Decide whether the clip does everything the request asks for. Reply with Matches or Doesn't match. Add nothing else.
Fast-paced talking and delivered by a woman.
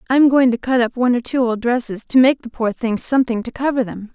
Matches